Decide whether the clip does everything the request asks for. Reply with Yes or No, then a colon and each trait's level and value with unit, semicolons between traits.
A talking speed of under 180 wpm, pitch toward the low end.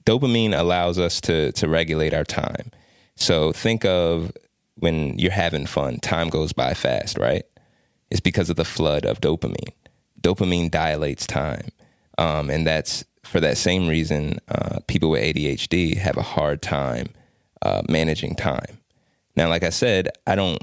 Yes: average, 155 wpm; very low, 85 Hz